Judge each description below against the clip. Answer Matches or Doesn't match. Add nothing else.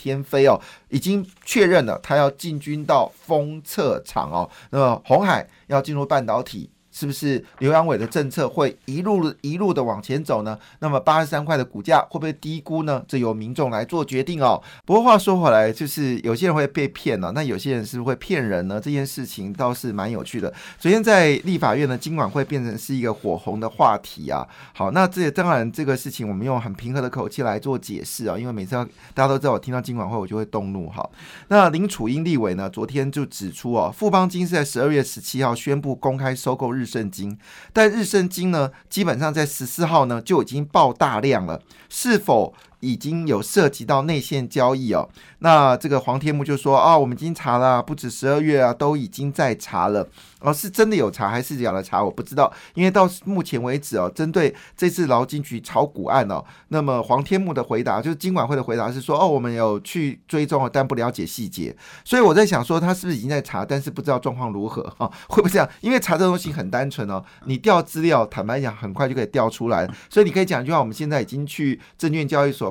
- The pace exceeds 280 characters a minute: Matches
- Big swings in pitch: Doesn't match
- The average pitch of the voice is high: Doesn't match